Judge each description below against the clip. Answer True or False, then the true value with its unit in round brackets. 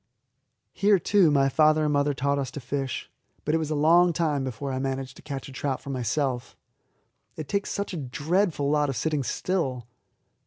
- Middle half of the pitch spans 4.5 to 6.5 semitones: False (2.9 semitones)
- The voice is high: False (145 Hz)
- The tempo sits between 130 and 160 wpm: False (195 wpm)